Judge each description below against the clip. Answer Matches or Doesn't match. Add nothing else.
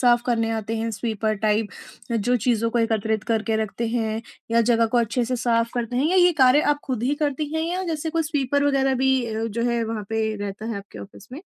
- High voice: Matches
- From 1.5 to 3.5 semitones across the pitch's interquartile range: Matches